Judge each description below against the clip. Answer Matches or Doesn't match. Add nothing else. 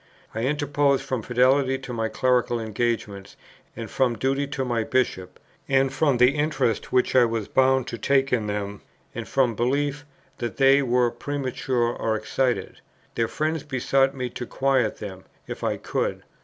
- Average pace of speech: Matches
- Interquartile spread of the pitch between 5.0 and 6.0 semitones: Doesn't match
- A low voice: Matches